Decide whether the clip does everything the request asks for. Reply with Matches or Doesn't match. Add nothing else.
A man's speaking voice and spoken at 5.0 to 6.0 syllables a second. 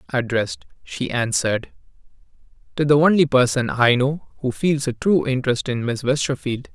Matches